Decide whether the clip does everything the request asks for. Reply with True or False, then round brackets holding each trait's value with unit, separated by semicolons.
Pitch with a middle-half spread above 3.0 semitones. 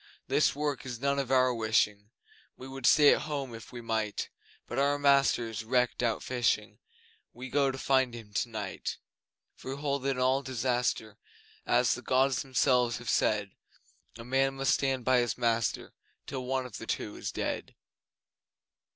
False (2.7 semitones)